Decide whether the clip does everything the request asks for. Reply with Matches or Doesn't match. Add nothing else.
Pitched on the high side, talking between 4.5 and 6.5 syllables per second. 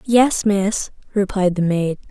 Doesn't match